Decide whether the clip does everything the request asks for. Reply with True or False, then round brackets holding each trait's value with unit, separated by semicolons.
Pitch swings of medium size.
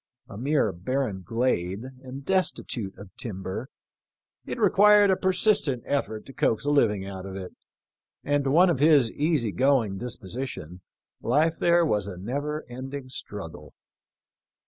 False (6.6 semitones)